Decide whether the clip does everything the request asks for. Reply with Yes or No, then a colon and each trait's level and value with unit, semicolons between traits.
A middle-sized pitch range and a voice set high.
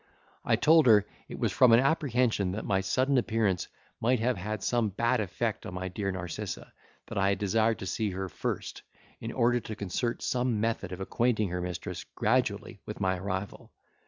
No: average, 3.9 semitones; low, 110 Hz